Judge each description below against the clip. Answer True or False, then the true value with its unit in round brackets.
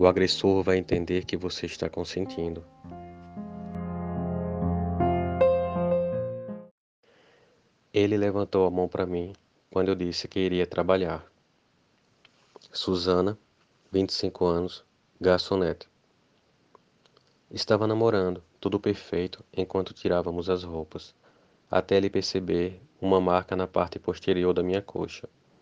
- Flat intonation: True (2.0 semitones)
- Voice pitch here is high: False (90 Hz)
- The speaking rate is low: True (100 wpm)